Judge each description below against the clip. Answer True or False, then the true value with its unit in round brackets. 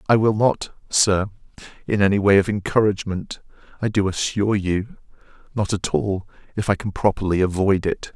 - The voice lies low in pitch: True (100 Hz)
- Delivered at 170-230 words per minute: False (160 wpm)